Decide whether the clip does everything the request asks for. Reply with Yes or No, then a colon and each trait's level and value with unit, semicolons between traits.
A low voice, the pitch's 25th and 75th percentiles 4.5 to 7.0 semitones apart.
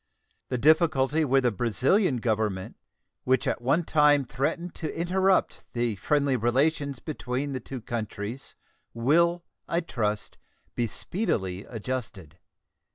Yes: low, 130 Hz; average, 5.1 semitones